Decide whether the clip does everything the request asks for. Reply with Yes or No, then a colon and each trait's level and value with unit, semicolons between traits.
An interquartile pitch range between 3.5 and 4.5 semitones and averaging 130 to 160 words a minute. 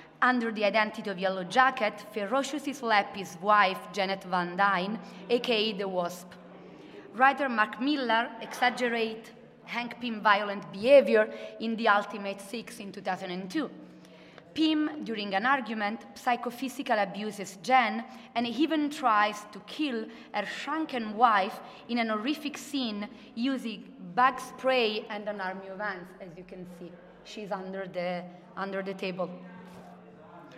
Yes: average, 4.0 semitones; average, 135 wpm